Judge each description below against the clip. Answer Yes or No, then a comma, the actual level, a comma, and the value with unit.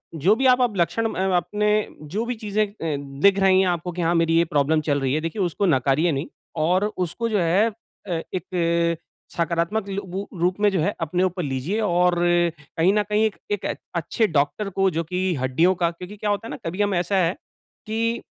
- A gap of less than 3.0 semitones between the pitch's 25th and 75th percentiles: No, average, 3.5 semitones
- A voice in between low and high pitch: Yes, medium, 180 Hz